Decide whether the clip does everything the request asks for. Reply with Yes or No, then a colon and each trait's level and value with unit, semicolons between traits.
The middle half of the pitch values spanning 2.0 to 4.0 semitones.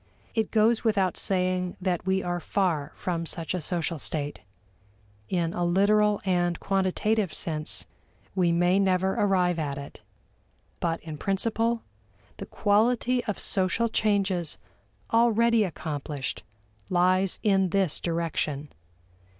Yes: average, 3.4 semitones